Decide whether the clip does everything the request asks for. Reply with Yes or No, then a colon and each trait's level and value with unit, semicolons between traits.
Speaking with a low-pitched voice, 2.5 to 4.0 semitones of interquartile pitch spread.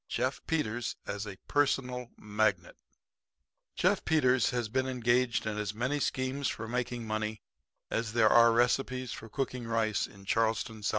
Yes: low, 115 Hz; average, 2.8 semitones